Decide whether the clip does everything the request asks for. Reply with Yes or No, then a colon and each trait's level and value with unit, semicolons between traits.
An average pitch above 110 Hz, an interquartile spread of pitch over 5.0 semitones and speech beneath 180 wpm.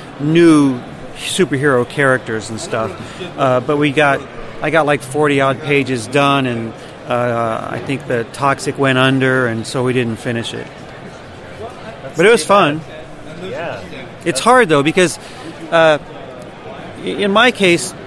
No: medium, 140 Hz; average, 3.9 semitones; average, 140 wpm